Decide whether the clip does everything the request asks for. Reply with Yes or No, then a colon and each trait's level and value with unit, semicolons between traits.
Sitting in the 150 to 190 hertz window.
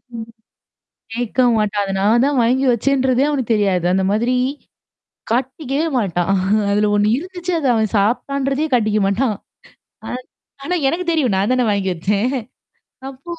No: high, 240 Hz